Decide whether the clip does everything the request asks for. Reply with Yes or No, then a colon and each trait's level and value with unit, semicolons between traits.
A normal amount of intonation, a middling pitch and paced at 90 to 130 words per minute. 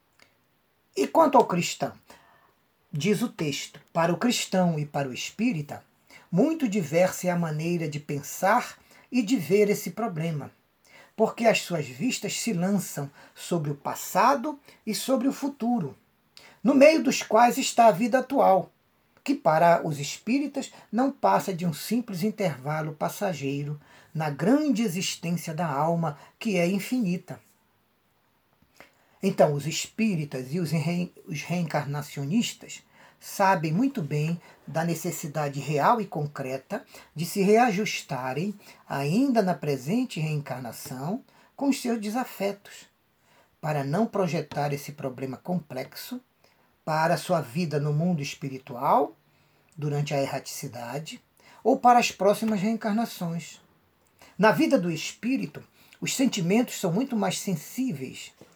No: wide, 7.2 semitones; medium, 180 Hz; average, 125 wpm